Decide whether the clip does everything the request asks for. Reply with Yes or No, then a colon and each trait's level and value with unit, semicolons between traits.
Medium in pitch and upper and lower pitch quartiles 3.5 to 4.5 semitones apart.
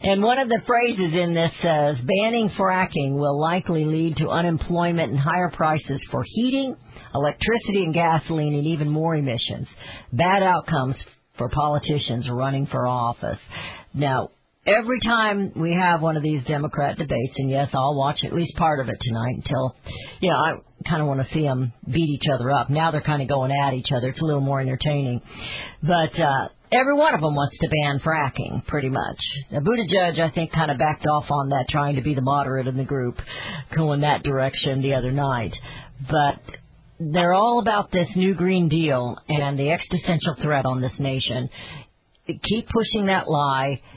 Yes: medium, 150 Hz; average, 4.0 semitones